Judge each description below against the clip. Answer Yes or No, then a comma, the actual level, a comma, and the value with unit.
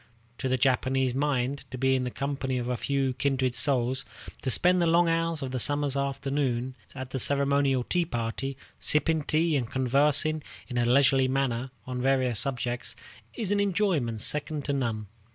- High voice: No, low, 135 Hz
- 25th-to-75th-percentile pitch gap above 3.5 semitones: No, narrow, 2.4 semitones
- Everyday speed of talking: Yes, average, 175 wpm